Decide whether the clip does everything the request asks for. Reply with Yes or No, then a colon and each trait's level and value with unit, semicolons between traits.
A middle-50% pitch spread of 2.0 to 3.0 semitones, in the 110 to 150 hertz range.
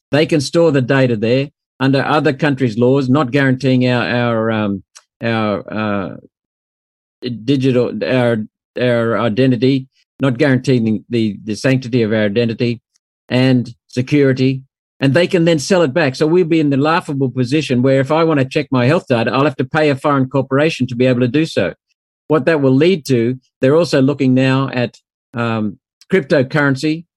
No: average, 3.4 semitones; low, 130 Hz